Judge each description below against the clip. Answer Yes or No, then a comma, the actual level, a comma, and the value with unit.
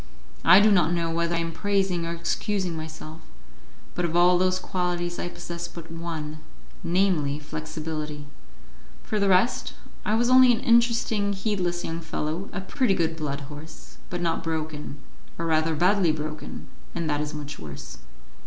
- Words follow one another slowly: No, average, 160 wpm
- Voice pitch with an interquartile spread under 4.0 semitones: Yes, average, 3.3 semitones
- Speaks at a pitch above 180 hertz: No, medium, 170 Hz